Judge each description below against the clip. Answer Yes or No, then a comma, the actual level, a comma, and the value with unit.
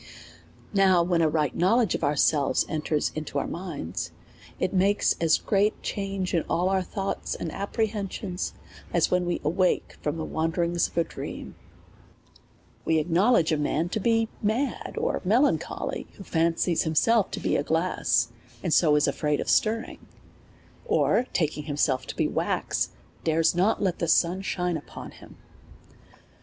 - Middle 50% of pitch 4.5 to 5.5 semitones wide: No, average, 3.8 semitones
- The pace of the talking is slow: No, average, 155 wpm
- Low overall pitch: No, medium, 175 Hz